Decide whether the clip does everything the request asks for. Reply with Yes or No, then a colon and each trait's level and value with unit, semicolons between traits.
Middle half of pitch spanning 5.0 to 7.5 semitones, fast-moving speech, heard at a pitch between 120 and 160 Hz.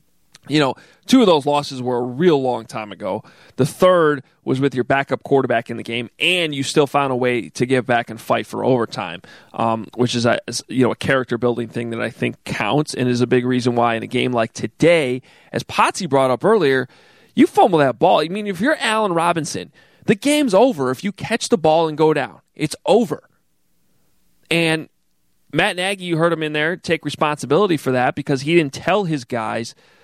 Yes: average, 5.3 semitones; fast, 210 wpm; medium, 140 Hz